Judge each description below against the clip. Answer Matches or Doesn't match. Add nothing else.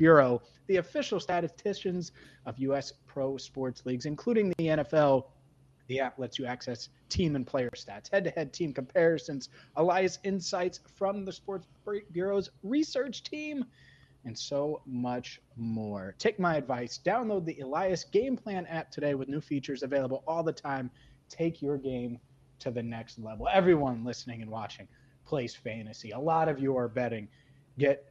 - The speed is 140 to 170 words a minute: Matches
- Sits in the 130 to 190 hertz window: Matches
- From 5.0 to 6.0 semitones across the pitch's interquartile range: Matches